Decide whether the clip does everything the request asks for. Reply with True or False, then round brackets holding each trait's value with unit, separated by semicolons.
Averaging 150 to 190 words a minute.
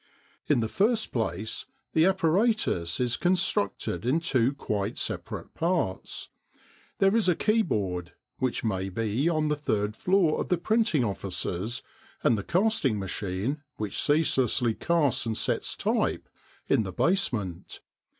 False (135 wpm)